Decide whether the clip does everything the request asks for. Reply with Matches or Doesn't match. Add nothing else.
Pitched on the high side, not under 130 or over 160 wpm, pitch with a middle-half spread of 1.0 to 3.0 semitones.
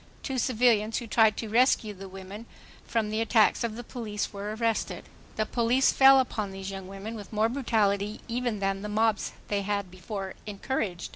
Doesn't match